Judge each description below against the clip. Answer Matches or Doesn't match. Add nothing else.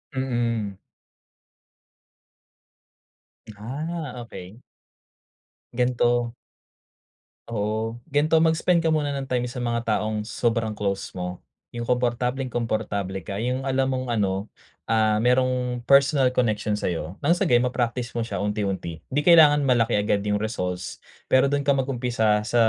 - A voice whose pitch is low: Matches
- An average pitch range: Matches